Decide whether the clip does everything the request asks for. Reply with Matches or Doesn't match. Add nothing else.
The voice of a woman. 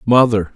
Doesn't match